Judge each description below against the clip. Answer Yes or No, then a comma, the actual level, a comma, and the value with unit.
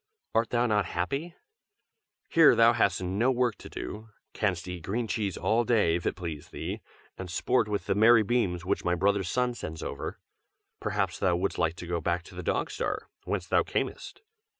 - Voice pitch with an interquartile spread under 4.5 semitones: No, average, 4.8 semitones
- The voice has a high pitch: No, low, 100 Hz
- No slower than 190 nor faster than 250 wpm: Yes, average, 195 wpm